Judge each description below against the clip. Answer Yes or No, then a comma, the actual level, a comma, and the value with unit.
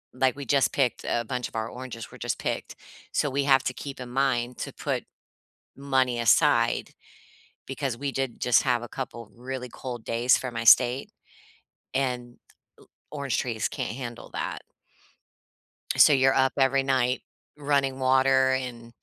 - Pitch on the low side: Yes, low, 130 Hz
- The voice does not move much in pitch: Yes, narrow, 1.9 semitones